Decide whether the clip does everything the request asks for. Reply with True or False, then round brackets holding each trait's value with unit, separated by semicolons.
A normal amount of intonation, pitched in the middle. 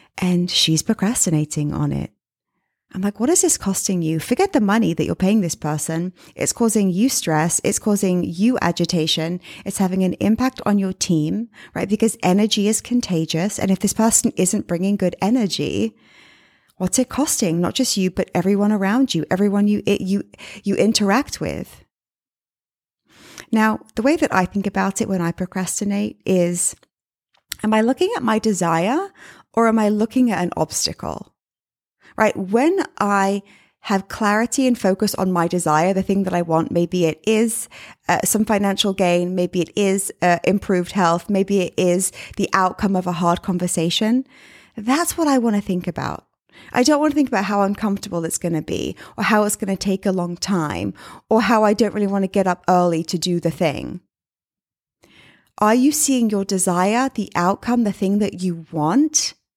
False (3.7 semitones; 195 Hz)